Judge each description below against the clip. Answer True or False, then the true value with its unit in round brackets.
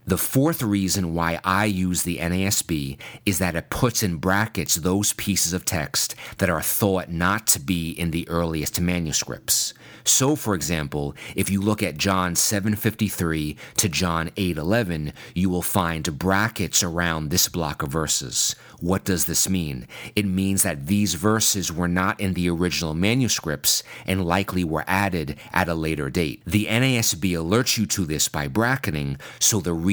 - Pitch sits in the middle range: False (95 Hz)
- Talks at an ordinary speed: True (165 wpm)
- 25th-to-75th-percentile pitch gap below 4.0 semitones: True (3.6 semitones)